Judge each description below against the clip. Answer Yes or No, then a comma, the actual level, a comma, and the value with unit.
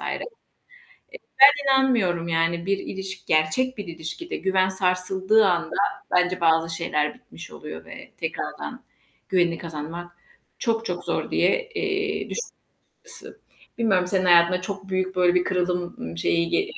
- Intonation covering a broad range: No, average, 2.8 semitones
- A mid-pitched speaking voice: Yes, medium, 180 Hz